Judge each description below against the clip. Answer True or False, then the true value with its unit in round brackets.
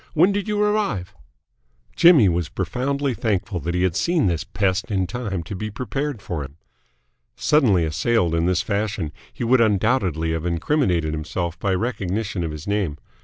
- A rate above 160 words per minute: True (170 wpm)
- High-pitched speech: False (100 Hz)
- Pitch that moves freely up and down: True (6.2 semitones)